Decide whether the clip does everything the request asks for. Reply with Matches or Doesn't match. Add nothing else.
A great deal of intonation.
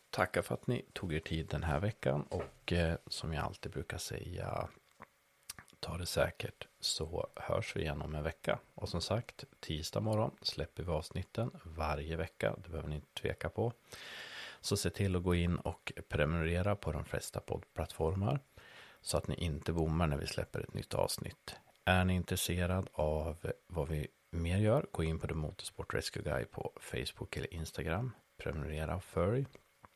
Doesn't match